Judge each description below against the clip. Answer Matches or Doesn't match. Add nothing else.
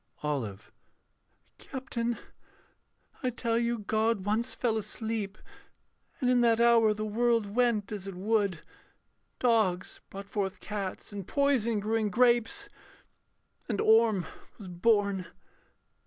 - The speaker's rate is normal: Doesn't match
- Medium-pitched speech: Doesn't match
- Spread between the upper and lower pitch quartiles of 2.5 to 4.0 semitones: Matches